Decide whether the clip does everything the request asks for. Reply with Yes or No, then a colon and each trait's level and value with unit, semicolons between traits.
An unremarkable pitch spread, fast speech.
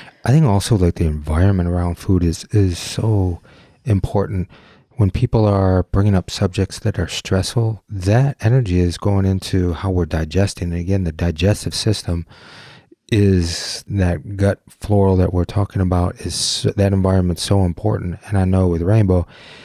No: average, 3.0 semitones; average, 160 wpm